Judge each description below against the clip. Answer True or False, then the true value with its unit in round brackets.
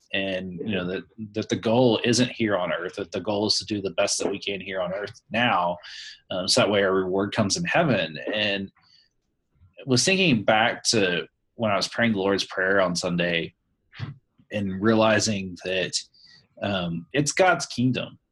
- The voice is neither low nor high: False (100 Hz)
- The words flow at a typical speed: True (185 wpm)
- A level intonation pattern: False (3.4 semitones)